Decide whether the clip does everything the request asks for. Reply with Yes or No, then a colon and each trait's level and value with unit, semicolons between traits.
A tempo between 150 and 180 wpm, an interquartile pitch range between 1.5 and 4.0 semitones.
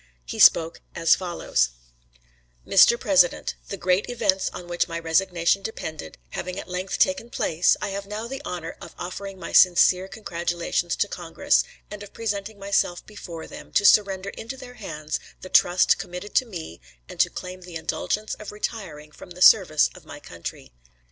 Yes: average, 170 wpm; average, 3.3 semitones